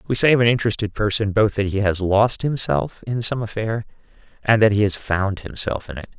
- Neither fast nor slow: No, fast, 225 wpm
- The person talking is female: No, male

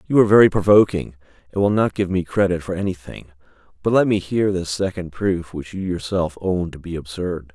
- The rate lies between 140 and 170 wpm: No, fast, 205 wpm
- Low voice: Yes, very low, 90 Hz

